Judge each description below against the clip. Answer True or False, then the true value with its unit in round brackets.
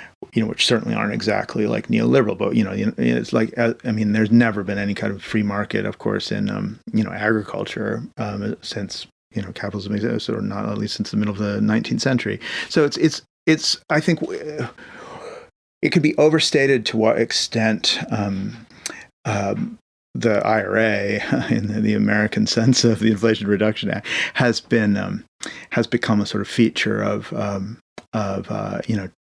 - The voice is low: True (110 Hz)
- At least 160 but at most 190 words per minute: True (180 wpm)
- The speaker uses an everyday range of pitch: False (2.3 semitones)